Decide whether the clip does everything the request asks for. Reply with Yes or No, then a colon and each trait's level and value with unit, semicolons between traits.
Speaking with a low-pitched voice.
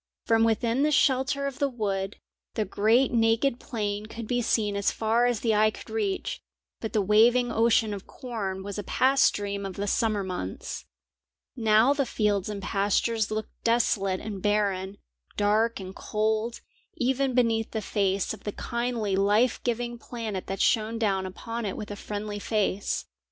No: high, 220 Hz